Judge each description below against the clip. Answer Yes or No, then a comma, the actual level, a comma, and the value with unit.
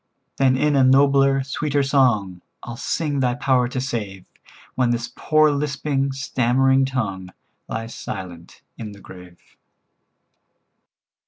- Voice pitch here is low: Yes, low, 130 Hz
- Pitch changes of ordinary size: Yes, average, 3.5 semitones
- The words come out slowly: Yes, slow, 120 wpm